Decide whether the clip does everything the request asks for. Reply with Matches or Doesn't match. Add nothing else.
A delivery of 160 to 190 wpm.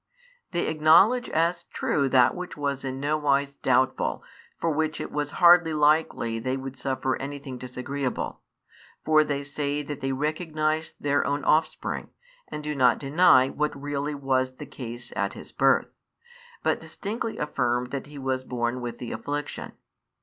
Matches